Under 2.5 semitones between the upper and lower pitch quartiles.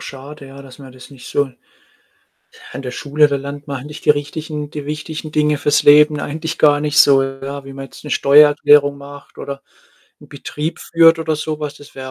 Yes: narrow, 1.5 semitones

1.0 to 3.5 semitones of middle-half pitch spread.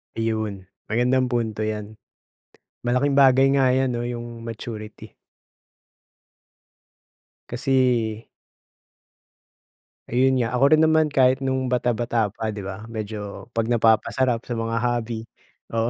Yes: narrow, 2.6 semitones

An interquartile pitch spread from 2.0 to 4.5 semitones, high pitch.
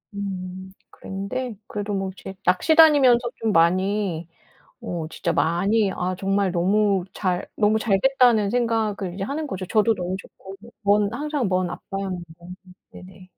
Yes: average, 3.2 semitones; high, 195 Hz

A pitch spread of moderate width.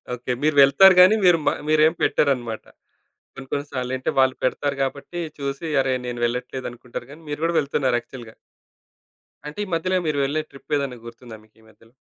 Yes: average, 3.5 semitones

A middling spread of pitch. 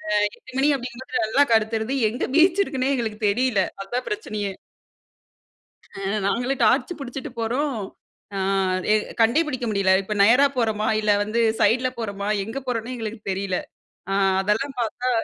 Yes: average, 3.5 semitones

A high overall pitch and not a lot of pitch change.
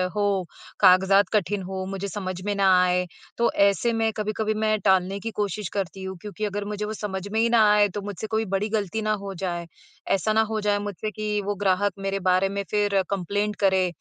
Yes: high, 205 Hz; narrow, 1.8 semitones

